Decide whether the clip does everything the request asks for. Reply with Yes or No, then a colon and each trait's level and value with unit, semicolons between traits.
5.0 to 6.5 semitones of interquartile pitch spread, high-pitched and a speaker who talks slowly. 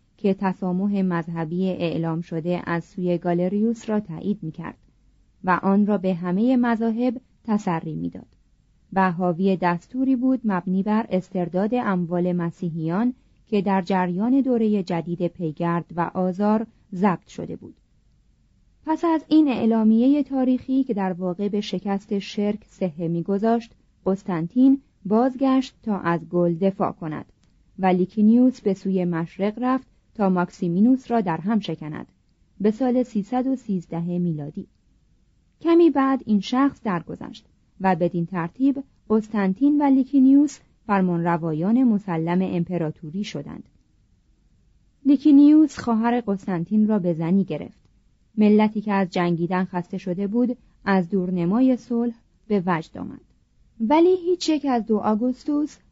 No: average, 5.3 semitones; high, 200 Hz; average, 125 wpm